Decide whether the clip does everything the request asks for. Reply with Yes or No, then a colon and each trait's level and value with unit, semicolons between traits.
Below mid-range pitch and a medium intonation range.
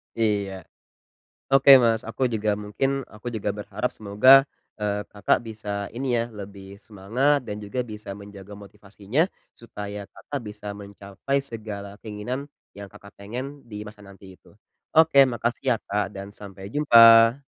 Yes: low, 105 Hz; average, 3.0 semitones